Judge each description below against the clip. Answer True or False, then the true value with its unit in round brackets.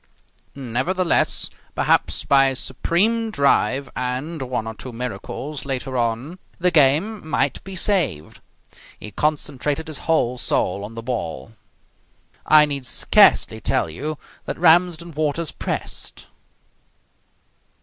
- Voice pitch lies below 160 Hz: True (140 Hz)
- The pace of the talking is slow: True (120 wpm)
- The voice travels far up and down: False (4.8 semitones)